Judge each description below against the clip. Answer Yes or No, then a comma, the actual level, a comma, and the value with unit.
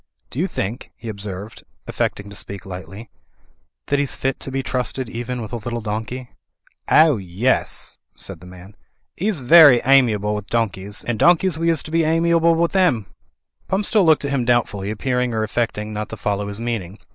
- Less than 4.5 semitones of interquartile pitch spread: No, wide, 5.4 semitones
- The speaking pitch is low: Yes, low, 120 Hz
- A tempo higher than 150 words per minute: Yes, average, 185 wpm